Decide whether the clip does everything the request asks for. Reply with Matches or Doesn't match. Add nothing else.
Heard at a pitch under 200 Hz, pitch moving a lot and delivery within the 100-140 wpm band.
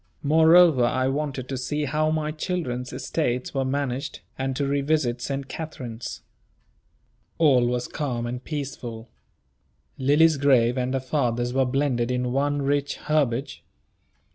Doesn't match